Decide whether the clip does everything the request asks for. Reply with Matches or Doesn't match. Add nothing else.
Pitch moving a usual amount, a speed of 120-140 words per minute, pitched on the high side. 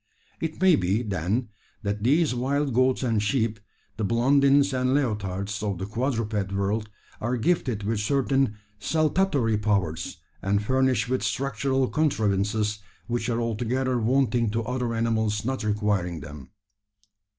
Doesn't match